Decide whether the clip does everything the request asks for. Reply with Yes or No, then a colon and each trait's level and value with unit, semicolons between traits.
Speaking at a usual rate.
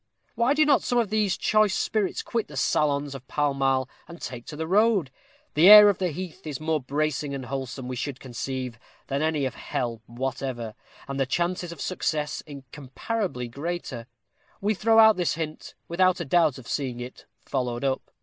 Yes: average, 190 wpm